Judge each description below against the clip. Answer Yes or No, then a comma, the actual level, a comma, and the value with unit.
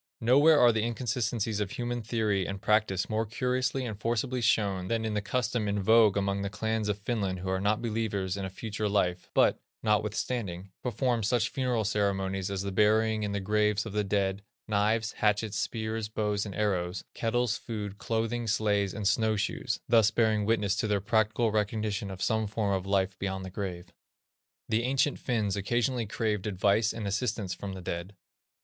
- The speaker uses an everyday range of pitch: No, narrow, 2.3 semitones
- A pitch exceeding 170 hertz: No, low, 105 Hz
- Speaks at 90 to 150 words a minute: No, average, 180 wpm